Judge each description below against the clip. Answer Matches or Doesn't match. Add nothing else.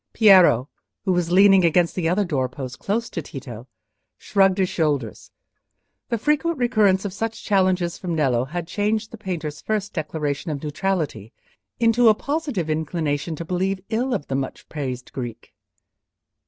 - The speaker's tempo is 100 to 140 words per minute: Doesn't match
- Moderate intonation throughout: Doesn't match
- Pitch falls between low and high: Matches